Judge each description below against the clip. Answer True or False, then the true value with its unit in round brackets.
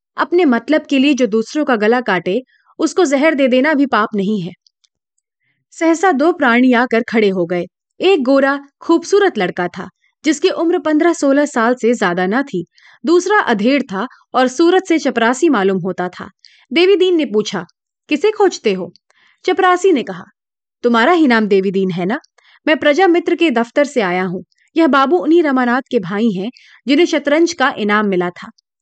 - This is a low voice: False (270 Hz)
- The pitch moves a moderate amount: False (7.7 semitones)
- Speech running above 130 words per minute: True (175 wpm)